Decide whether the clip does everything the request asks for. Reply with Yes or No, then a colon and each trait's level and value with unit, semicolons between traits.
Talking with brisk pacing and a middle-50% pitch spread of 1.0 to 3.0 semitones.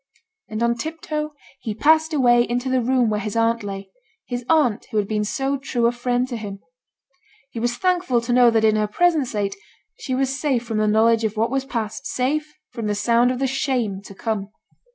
No: fast, 215 wpm; average, 3.6 semitones